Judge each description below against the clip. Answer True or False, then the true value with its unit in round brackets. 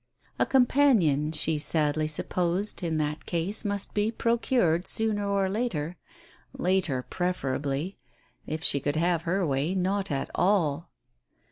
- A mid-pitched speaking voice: True (175 Hz)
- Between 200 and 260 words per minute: False (135 wpm)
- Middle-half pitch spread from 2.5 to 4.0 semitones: False (4.7 semitones)